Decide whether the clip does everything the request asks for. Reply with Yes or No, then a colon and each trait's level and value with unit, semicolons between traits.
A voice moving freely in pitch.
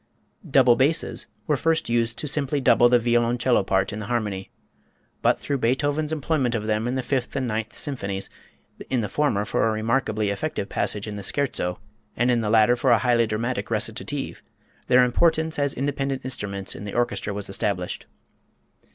No: average, 4.1 semitones